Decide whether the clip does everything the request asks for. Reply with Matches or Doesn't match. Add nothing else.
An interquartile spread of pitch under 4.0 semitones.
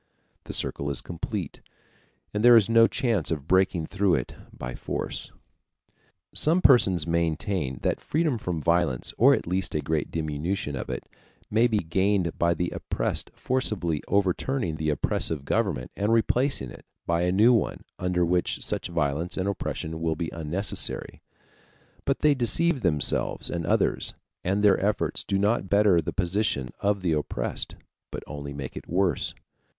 Doesn't match